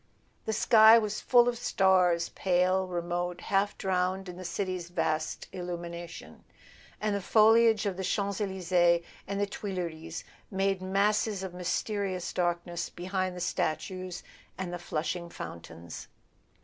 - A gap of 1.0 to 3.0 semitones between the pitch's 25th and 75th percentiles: Yes, narrow, 2.4 semitones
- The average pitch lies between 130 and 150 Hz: No, medium, 185 Hz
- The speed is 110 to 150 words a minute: Yes, slow, 135 wpm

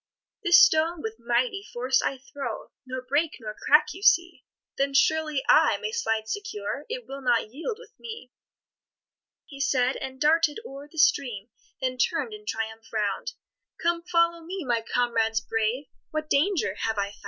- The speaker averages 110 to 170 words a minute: Yes, average, 165 wpm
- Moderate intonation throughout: No, wide, 6.1 semitones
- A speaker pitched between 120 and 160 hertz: No, very high, 275 Hz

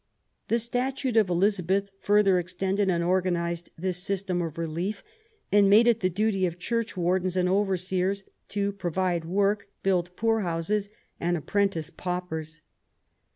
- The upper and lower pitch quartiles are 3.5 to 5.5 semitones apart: No, narrow, 2.4 semitones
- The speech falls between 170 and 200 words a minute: No, average, 140 wpm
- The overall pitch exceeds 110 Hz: Yes, medium, 185 Hz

